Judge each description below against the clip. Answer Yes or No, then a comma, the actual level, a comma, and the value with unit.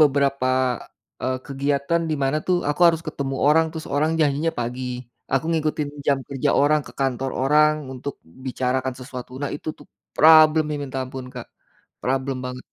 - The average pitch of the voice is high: No, medium, 140 Hz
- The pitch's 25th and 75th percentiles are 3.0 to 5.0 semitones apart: No, narrow, 2.6 semitones